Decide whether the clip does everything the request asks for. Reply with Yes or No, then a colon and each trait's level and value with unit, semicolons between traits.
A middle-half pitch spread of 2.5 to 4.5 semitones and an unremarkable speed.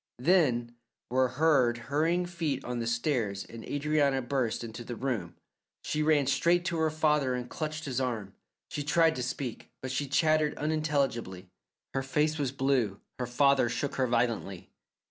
Yes: average, 4.2 semitones; average, 165 wpm